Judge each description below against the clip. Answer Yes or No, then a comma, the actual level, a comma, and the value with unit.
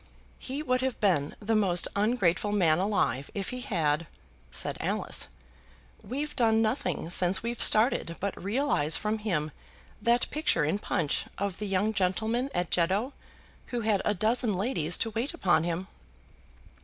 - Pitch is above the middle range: Yes, high, 205 Hz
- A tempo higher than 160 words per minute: No, average, 155 wpm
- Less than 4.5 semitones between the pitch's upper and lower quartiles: No, average, 4.9 semitones